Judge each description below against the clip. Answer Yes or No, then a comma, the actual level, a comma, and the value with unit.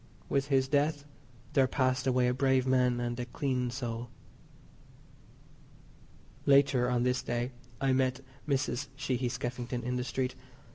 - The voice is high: No, low, 130 Hz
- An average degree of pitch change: No, narrow, 1.4 semitones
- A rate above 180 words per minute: No, average, 140 wpm